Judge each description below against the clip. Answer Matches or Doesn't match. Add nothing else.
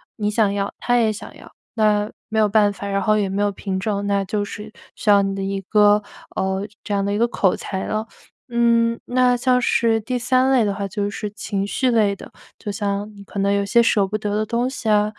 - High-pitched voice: Matches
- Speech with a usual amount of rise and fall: Doesn't match